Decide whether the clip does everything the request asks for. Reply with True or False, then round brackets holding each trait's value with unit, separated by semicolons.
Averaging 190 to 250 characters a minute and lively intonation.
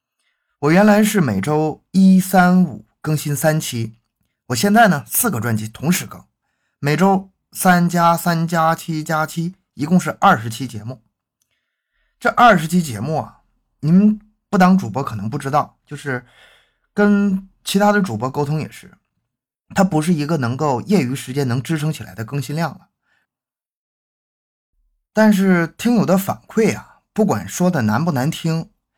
True (220 characters per minute; 6.6 semitones)